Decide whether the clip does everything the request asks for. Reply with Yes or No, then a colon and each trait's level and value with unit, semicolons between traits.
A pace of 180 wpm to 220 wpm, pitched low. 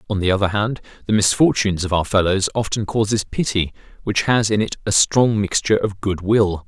Yes: average, 200 wpm; low, 105 Hz